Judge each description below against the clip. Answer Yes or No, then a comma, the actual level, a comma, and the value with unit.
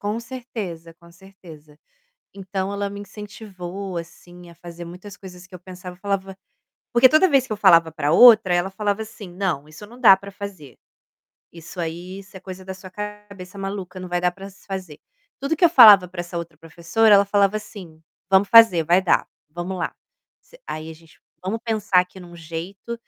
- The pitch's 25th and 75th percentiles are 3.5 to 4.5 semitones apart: No, average, 2.9 semitones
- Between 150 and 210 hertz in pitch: Yes, high, 190 Hz